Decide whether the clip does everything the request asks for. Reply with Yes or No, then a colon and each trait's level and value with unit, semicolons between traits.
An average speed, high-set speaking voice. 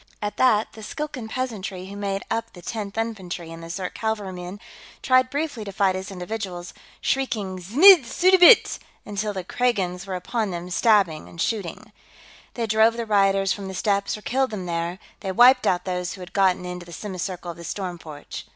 Yes: average, 190 wpm; high, 200 Hz